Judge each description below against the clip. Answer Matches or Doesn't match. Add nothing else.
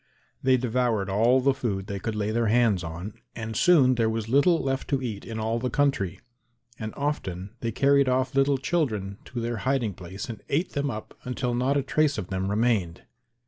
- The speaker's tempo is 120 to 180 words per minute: Doesn't match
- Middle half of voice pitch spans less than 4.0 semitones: Doesn't match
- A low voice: Matches